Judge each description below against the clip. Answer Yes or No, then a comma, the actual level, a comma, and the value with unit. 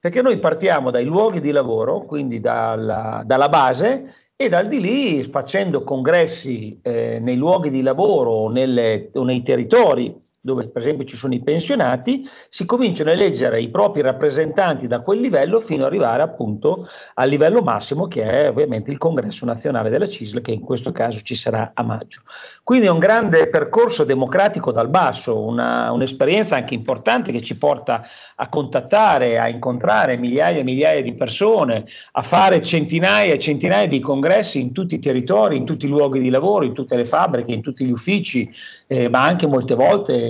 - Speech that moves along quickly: Yes, fast, 180 wpm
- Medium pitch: Yes, medium, 145 Hz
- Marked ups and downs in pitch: Yes, wide, 7.6 semitones